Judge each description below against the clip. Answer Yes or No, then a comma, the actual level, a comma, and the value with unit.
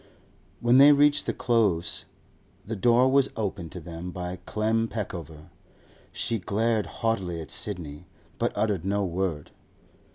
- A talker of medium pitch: No, low, 100 Hz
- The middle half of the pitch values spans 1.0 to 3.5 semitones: No, average, 4.6 semitones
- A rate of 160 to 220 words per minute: No, slow, 135 wpm